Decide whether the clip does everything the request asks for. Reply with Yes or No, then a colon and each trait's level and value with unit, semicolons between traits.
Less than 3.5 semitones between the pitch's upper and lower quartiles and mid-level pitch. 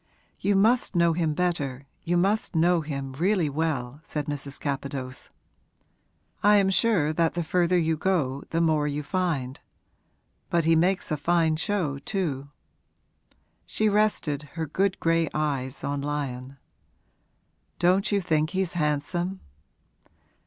No: average, 3.9 semitones; medium, 160 Hz